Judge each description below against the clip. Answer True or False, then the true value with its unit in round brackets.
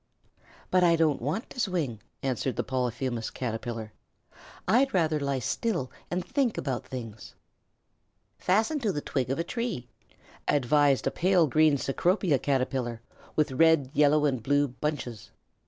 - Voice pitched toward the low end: False (145 Hz)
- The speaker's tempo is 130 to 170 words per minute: True (140 wpm)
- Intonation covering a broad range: False (4.9 semitones)